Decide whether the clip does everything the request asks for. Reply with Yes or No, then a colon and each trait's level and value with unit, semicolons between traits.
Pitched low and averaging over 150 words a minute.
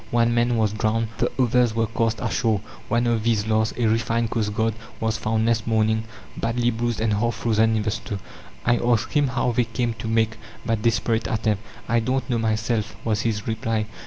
Yes: low, 115 Hz; average, 195 wpm